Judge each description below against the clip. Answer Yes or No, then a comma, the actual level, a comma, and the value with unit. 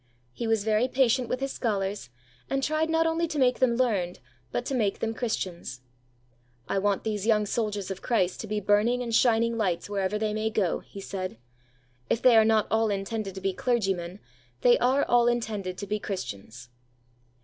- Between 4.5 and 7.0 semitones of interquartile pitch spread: No, average, 3.7 semitones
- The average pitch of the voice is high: Yes, high, 215 Hz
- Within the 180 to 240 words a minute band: Yes, average, 190 wpm